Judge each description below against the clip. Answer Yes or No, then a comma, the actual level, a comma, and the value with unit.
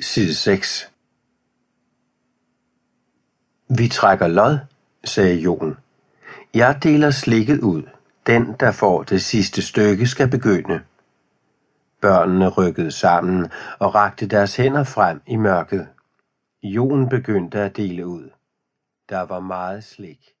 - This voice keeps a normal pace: No, slow, 110 wpm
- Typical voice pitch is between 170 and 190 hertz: No, low, 105 Hz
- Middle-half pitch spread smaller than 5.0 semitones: No, average, 5.3 semitones